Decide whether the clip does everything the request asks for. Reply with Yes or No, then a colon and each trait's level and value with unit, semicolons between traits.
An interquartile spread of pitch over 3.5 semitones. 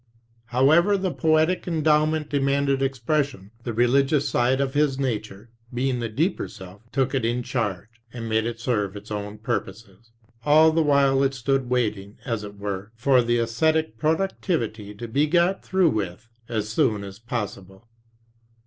Yes: average, 5.1 semitones